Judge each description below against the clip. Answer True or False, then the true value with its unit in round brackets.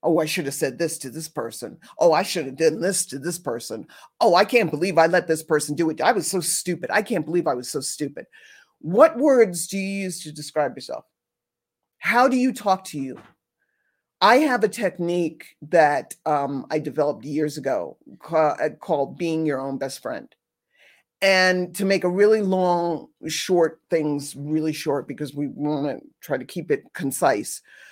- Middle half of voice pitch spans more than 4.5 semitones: False (4.0 semitones)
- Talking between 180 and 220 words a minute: True (190 wpm)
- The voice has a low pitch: False (165 Hz)